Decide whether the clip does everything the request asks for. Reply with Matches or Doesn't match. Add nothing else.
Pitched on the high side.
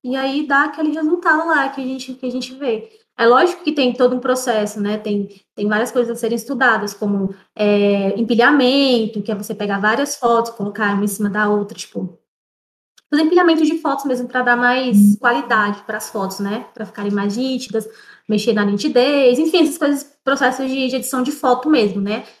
Matches